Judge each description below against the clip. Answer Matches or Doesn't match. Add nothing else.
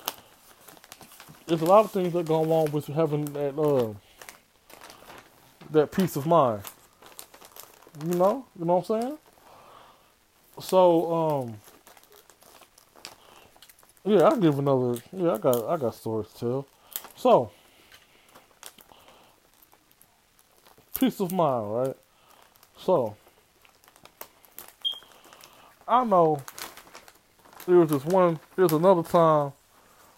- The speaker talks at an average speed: Doesn't match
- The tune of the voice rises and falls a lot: Doesn't match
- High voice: Doesn't match